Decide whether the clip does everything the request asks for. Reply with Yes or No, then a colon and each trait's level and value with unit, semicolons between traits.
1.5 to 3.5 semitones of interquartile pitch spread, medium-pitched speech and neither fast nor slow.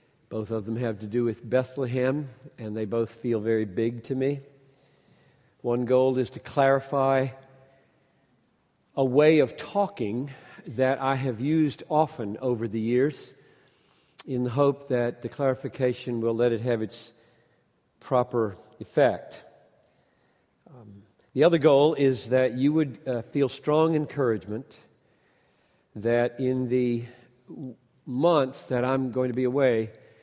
No: narrow, 2.5 semitones; low, 130 Hz; average, 130 wpm